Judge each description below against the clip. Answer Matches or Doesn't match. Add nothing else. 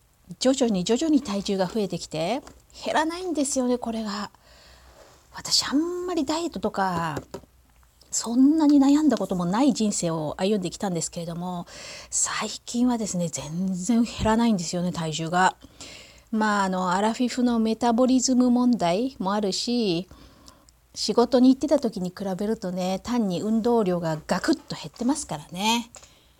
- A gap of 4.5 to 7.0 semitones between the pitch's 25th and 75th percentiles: Matches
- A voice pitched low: Doesn't match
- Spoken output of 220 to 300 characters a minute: Doesn't match